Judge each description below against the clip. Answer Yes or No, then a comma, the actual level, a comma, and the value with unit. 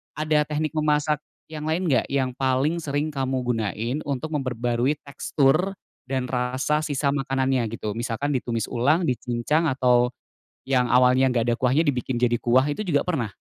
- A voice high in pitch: No, low, 135 Hz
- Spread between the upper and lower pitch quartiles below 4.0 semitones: Yes, average, 3.3 semitones